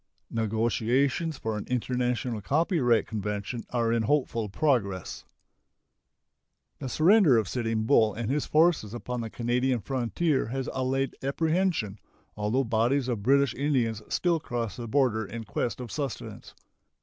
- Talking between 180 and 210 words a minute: No, slow, 135 wpm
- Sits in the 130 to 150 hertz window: No, low, 120 Hz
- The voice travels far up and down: No, average, 3.7 semitones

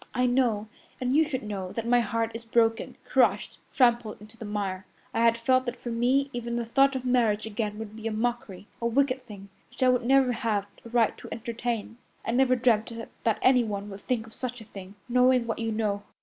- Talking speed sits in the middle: No, fast, 220 wpm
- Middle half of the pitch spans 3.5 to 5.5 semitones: No, narrow, 2.5 semitones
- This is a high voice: Yes, high, 230 Hz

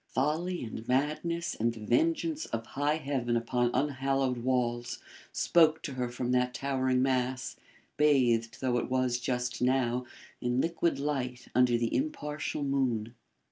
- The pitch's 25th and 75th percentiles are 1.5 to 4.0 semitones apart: Yes, average, 3.1 semitones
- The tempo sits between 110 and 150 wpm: Yes, average, 140 wpm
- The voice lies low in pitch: Yes, low, 130 Hz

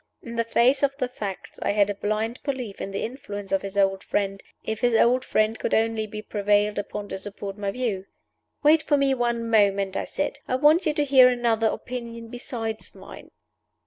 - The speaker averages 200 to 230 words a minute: Yes, fast, 205 wpm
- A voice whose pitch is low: No, high, 225 Hz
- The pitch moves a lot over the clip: No, average, 3.6 semitones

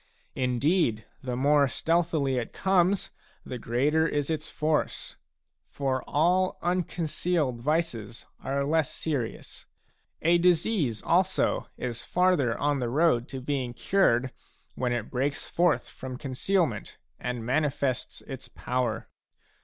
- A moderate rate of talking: No, slow, 120 wpm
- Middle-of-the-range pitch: Yes, medium, 145 Hz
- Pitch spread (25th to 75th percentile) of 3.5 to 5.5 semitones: Yes, average, 4.9 semitones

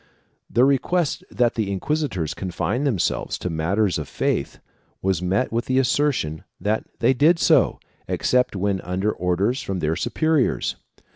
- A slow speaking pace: No, average, 150 wpm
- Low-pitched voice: Yes, low, 105 Hz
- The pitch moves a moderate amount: No, wide, 6.4 semitones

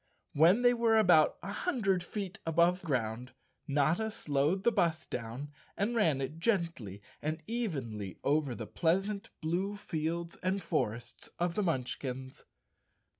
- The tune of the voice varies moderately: No, wide, 6.2 semitones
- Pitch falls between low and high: Yes, medium, 165 Hz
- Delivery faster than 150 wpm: No, slow, 135 wpm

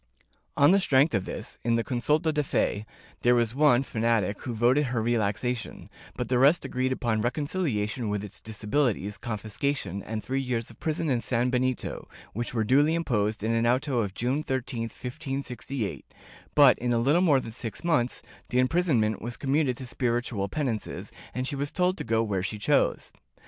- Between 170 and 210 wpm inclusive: Yes, average, 180 wpm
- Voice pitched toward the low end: Yes, low, 120 Hz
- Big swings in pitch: No, average, 3.8 semitones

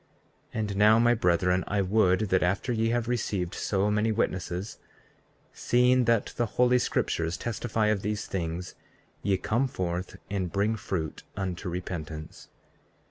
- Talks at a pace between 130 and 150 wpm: Yes, average, 145 wpm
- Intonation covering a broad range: No, average, 3.7 semitones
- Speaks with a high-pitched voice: No, low, 100 Hz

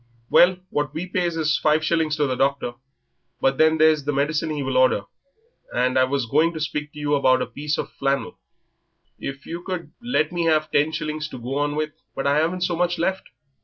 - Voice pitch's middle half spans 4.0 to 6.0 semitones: No, average, 2.7 semitones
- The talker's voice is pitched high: No, medium, 150 Hz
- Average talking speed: No, fast, 215 wpm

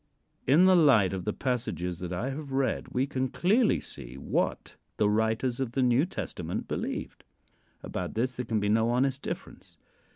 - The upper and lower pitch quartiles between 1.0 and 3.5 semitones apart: No, average, 4.6 semitones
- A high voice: No, low, 125 Hz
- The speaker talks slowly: No, average, 175 wpm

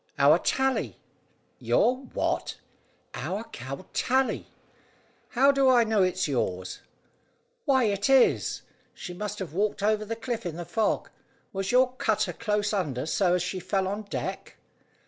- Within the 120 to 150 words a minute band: Yes, average, 145 wpm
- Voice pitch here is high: Yes, high, 205 Hz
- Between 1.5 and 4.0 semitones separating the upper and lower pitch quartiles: No, average, 4.8 semitones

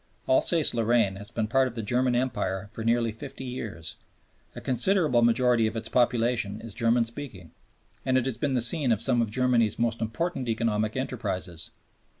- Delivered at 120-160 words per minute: No, average, 175 wpm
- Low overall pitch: Yes, low, 120 Hz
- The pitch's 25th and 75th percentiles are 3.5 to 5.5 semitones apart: No, narrow, 2.5 semitones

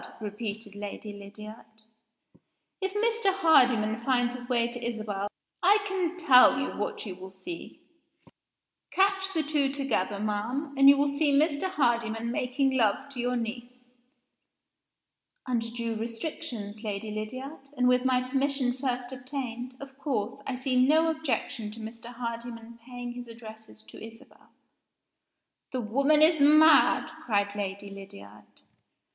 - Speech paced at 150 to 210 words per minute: No, average, 140 wpm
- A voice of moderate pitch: No, high, 245 Hz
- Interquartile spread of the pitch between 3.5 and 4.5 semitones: Yes, average, 4.1 semitones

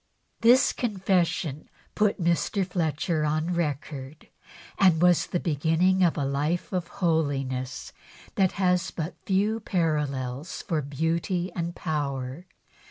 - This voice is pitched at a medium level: Yes, medium, 165 Hz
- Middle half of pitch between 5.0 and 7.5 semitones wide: No, average, 3.7 semitones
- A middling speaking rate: No, slow, 115 wpm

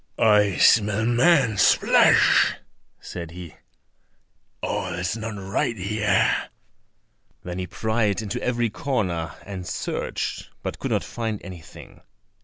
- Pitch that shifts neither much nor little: Yes, average, 3.6 semitones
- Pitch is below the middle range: Yes, low, 105 Hz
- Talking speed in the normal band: No, slow, 115 wpm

